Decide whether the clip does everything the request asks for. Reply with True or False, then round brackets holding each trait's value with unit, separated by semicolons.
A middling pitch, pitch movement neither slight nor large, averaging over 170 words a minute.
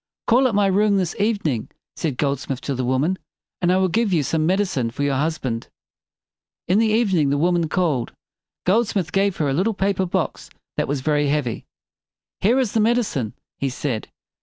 False (175 Hz; 6.2 semitones; 200 wpm)